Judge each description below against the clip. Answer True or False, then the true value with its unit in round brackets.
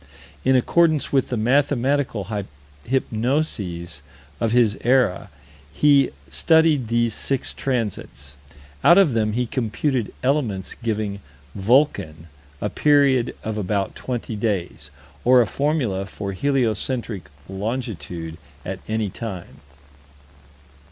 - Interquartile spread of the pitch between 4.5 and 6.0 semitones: True (5.1 semitones)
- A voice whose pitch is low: True (115 Hz)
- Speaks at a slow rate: True (105 wpm)